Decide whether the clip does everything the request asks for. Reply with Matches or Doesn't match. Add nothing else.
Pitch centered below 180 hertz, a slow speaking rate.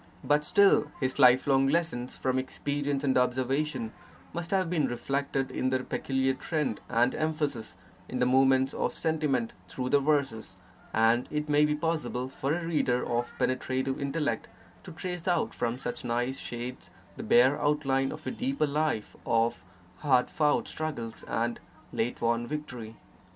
Doesn't match